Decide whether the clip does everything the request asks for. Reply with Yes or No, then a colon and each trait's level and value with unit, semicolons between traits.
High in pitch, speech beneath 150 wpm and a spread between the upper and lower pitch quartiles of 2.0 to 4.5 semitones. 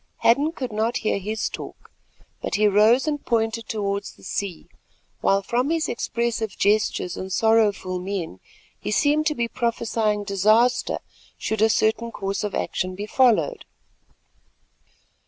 Yes: high, 220 Hz; average, 140 wpm; average, 2.8 semitones